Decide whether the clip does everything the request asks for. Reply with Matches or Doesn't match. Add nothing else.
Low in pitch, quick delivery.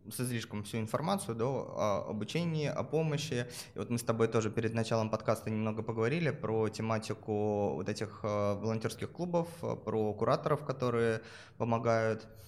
Doesn't match